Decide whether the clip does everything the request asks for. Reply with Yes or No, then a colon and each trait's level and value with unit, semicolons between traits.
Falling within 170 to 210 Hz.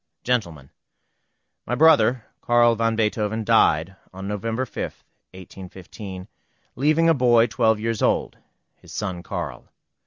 No: low, 110 Hz